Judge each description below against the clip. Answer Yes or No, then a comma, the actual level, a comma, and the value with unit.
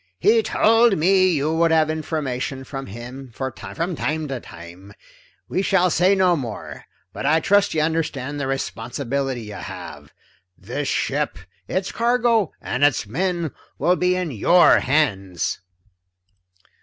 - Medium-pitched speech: Yes, medium, 155 Hz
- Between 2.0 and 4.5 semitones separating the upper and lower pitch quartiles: No, wide, 5.6 semitones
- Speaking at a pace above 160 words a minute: No, average, 145 wpm